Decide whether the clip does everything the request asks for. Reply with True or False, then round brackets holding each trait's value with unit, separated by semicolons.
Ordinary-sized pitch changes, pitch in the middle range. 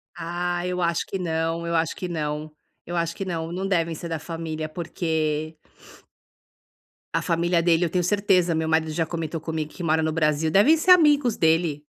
False (1.8 semitones; 165 Hz)